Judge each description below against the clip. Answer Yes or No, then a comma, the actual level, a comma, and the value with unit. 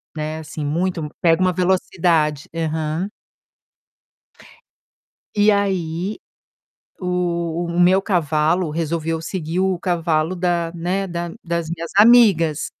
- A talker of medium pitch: Yes, medium, 170 Hz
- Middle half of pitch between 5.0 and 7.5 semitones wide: No, narrow, 2.4 semitones